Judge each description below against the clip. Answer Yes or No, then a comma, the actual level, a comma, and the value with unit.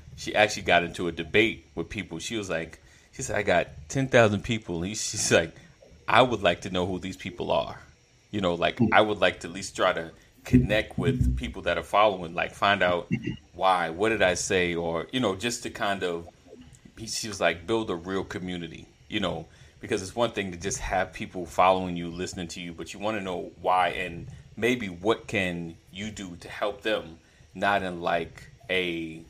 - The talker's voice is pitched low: Yes, very low, 90 Hz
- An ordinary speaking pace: No, fast, 210 wpm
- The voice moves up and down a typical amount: Yes, average, 4.0 semitones